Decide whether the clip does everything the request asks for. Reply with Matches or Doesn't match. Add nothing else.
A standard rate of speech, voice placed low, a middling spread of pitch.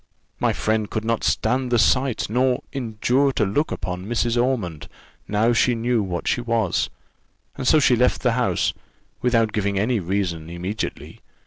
Matches